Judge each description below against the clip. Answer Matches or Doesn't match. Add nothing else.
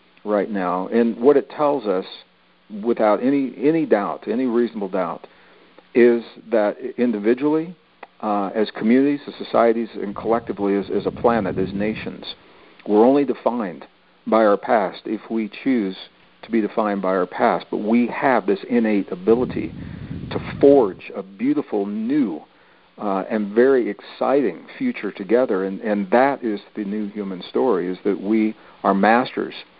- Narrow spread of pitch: Doesn't match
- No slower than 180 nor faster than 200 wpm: Doesn't match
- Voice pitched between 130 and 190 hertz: Doesn't match